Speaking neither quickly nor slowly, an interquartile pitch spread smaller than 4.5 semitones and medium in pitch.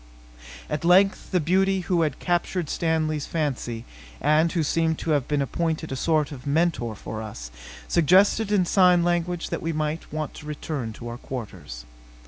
Yes: average, 175 wpm; average, 3.9 semitones; medium, 155 Hz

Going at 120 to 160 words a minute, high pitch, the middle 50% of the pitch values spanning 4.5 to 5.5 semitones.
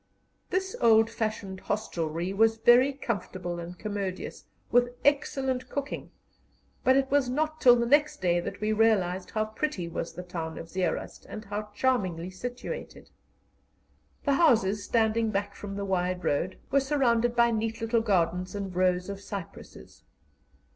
Yes: average, 150 wpm; high, 215 Hz; average, 4.9 semitones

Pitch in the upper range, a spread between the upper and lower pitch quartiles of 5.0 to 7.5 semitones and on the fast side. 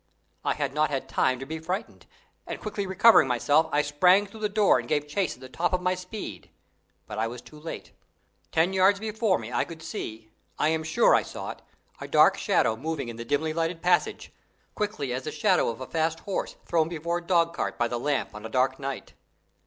No: medium, 160 Hz; wide, 5.5 semitones; fast, 220 wpm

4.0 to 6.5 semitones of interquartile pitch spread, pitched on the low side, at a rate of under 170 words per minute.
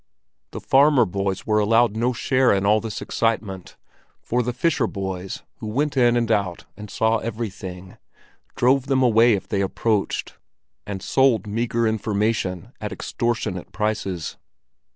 No: average, 3.4 semitones; low, 110 Hz; average, 140 wpm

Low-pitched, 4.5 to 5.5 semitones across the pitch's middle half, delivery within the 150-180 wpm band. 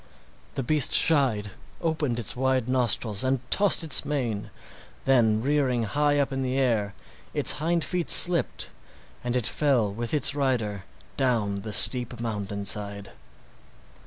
No: low, 125 Hz; average, 4.8 semitones; average, 140 wpm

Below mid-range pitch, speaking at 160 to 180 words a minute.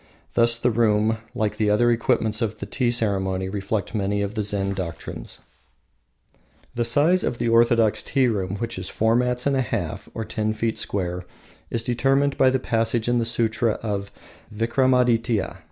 Yes: low, 115 Hz; average, 170 wpm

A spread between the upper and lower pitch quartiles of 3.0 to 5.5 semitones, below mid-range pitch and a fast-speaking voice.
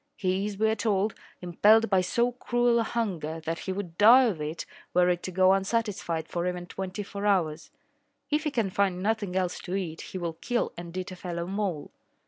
No: average, 3.4 semitones; high, 190 Hz; fast, 210 wpm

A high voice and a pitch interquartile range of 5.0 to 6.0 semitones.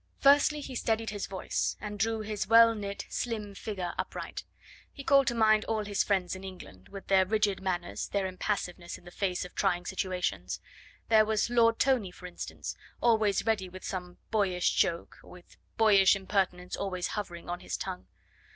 No: high, 200 Hz; average, 3.3 semitones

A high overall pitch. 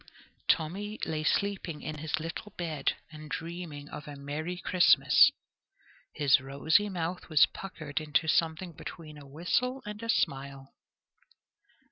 No: medium, 160 Hz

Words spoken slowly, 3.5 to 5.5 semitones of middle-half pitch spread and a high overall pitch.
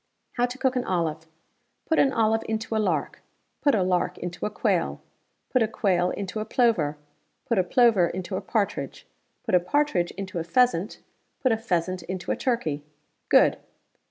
No: average, 180 wpm; average, 5.0 semitones; high, 195 Hz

